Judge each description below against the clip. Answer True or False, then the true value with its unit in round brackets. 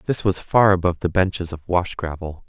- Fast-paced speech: True (220 wpm)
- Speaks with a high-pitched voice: False (90 Hz)